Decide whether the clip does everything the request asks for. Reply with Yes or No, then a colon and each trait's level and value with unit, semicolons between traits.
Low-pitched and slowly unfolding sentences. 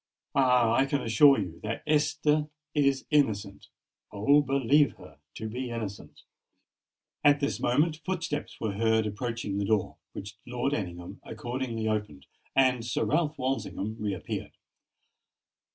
Yes: low, 120 Hz; slow, 130 wpm